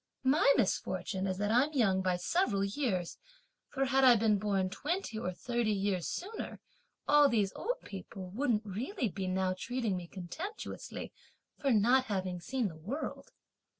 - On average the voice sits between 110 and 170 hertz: No, high, 210 Hz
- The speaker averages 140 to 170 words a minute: Yes, average, 155 wpm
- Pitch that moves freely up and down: Yes, wide, 5.8 semitones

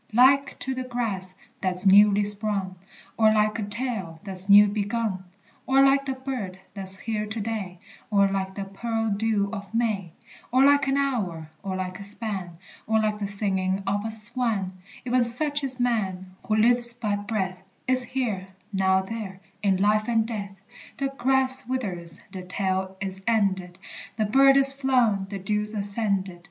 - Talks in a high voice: Yes, high, 210 Hz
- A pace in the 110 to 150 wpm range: No, average, 170 wpm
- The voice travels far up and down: No, average, 3.8 semitones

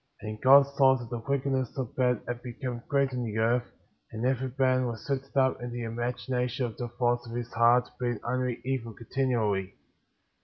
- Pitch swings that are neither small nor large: No, narrow, 1.9 semitones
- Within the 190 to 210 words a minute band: Yes, average, 195 wpm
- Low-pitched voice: Yes, low, 125 Hz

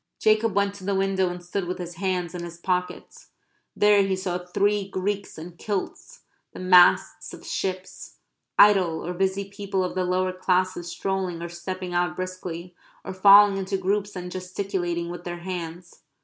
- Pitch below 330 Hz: Yes, medium, 185 Hz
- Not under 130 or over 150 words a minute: No, average, 170 wpm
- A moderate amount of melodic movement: No, narrow, 1.7 semitones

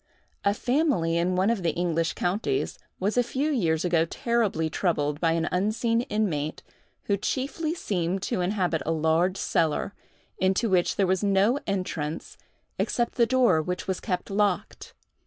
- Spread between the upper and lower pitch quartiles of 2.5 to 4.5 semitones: No, average, 5.0 semitones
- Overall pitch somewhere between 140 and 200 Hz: Yes, medium, 185 Hz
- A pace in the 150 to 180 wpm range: Yes, average, 155 wpm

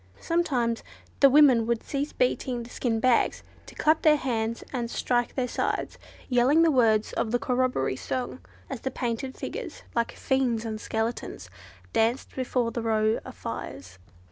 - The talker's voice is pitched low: No, high, 245 Hz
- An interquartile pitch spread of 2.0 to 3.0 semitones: Yes, average, 2.7 semitones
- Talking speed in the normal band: Yes, average, 160 wpm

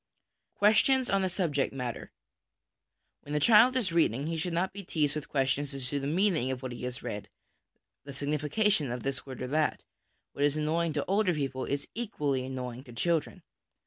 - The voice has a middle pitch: Yes, medium, 145 Hz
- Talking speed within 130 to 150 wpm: No, average, 190 wpm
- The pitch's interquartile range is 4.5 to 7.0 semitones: Yes, average, 4.9 semitones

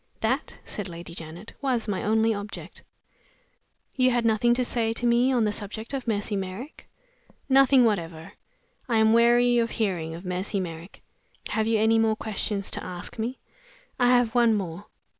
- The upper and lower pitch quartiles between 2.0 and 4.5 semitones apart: Yes, average, 3.7 semitones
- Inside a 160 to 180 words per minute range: Yes, average, 170 wpm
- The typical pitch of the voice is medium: No, high, 220 Hz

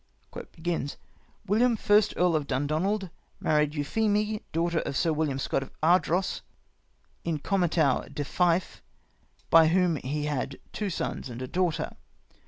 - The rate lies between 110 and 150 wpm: Yes, slow, 135 wpm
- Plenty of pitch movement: No, average, 4.2 semitones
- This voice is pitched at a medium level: Yes, medium, 165 Hz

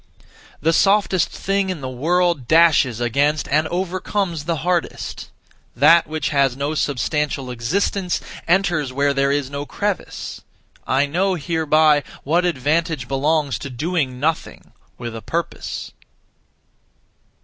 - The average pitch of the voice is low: No, medium, 155 Hz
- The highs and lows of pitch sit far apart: No, average, 3.9 semitones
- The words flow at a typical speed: No, slow, 125 wpm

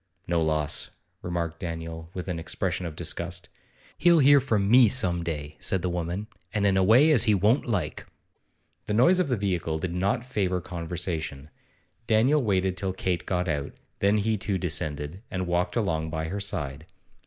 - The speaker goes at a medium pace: Yes, average, 175 wpm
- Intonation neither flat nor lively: Yes, average, 4.0 semitones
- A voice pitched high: No, very low, 90 Hz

